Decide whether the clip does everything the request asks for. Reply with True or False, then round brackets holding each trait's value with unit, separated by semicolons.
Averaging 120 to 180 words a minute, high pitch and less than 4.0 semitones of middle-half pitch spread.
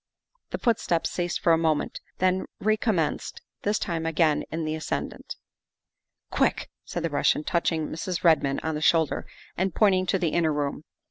False (175 wpm; 165 Hz; 2.8 semitones)